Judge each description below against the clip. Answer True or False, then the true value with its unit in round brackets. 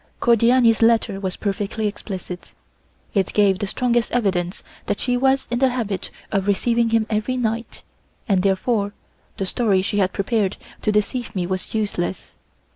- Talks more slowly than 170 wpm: True (155 wpm)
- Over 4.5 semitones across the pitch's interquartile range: False (3.3 semitones)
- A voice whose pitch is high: True (210 Hz)